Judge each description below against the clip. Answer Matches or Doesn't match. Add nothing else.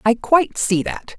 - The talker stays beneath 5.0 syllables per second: Matches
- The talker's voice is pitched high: Matches